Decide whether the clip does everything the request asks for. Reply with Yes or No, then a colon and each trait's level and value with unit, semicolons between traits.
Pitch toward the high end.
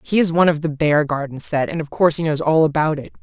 No: medium, 155 Hz